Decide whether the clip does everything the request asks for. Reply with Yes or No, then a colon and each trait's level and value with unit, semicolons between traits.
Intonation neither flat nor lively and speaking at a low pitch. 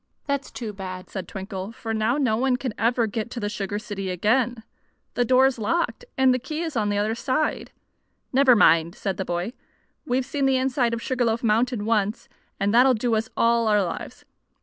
No: average, 3.7 semitones; high, 230 Hz